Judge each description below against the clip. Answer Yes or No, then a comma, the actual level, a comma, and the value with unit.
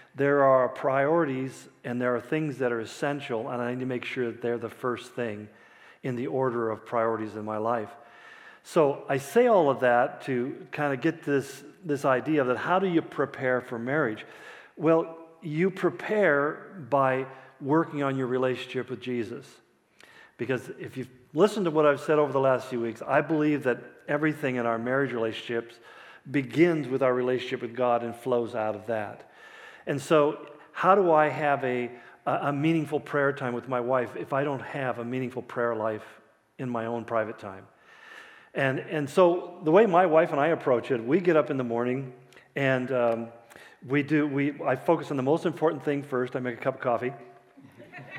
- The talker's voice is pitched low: Yes, low, 130 Hz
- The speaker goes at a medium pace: Yes, average, 195 wpm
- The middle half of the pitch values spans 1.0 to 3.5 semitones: No, average, 3.9 semitones